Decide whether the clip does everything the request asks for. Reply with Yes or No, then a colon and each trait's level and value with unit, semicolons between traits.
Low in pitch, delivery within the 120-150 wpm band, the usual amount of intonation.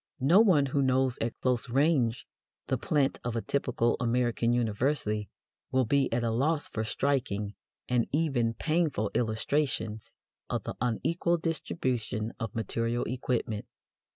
Yes: low, 125 Hz; slow, 135 wpm; average, 3.7 semitones